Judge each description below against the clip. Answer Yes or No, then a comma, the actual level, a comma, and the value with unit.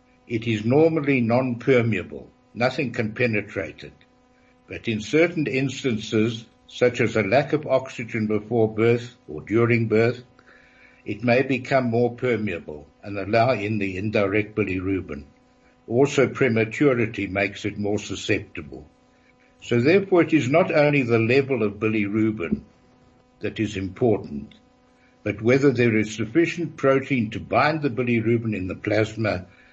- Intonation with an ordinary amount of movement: Yes, average, 3.7 semitones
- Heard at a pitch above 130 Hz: No, low, 115 Hz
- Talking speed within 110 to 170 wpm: Yes, slow, 135 wpm